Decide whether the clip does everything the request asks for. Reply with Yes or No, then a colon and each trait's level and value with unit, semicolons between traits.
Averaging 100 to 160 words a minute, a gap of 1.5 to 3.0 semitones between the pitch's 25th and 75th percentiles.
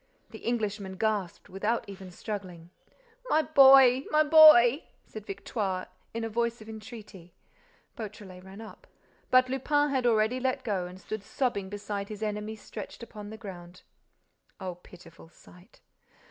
No: average, 140 wpm; average, 4.0 semitones